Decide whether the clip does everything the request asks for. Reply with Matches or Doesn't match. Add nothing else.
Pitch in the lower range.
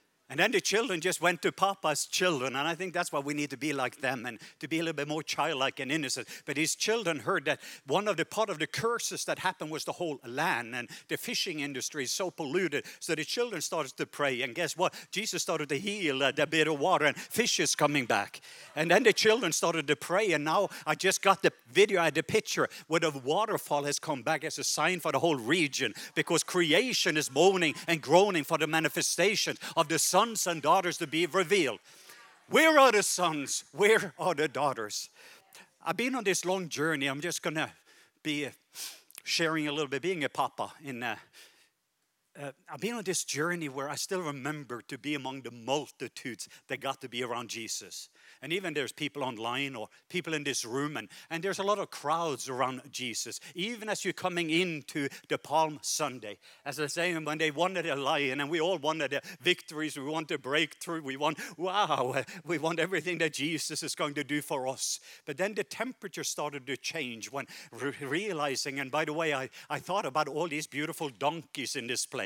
Doesn't match